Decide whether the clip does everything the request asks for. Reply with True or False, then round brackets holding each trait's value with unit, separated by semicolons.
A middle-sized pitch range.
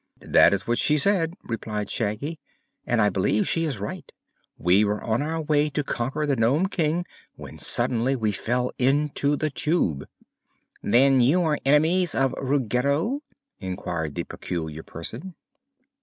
False (6.2 semitones)